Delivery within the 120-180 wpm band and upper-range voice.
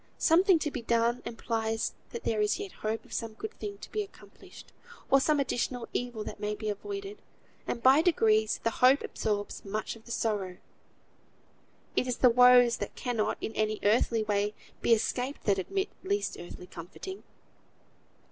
Yes: average, 170 wpm; high, 235 Hz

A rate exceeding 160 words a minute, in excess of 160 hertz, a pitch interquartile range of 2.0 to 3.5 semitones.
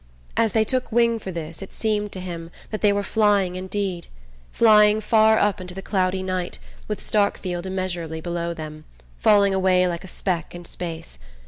Yes: average, 180 wpm; high, 190 Hz; average, 3.1 semitones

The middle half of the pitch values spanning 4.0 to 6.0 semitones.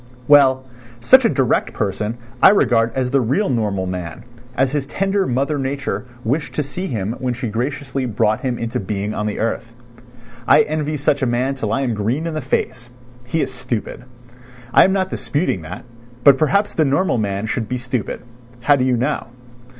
Yes: average, 4.3 semitones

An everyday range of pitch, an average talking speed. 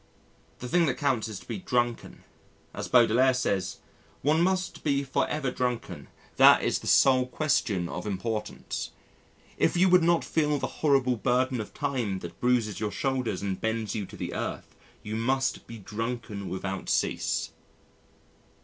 Yes: average, 4.1 semitones; average, 160 wpm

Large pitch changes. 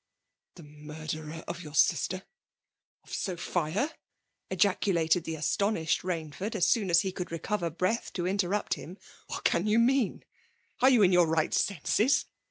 No: average, 4.1 semitones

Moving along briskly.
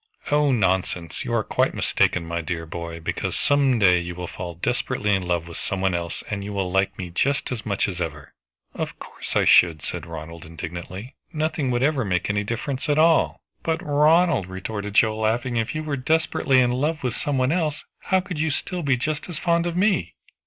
Yes: fast, 210 wpm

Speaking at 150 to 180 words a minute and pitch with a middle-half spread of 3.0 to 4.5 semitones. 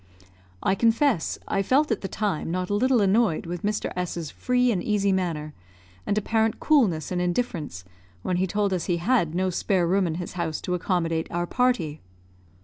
No: average, 190 wpm; average, 4.1 semitones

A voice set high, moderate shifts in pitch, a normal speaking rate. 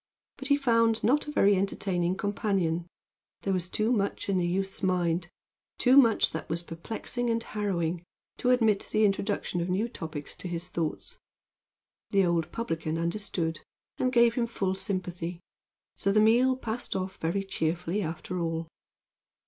Yes: high, 195 Hz; average, 4.5 semitones; average, 155 wpm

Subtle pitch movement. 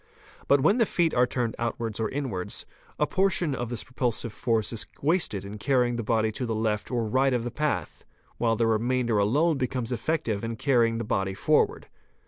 No: average, 3.4 semitones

